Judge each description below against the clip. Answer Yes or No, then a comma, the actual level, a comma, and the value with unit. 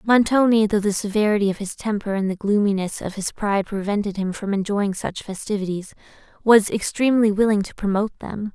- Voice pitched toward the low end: No, high, 205 Hz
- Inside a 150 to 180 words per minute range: Yes, average, 175 wpm